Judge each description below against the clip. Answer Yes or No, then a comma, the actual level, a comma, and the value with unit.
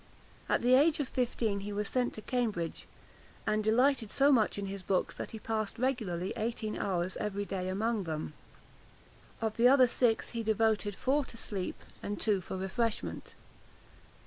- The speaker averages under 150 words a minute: No, average, 170 wpm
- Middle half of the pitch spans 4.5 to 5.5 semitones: No, average, 3.4 semitones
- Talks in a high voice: Yes, high, 215 Hz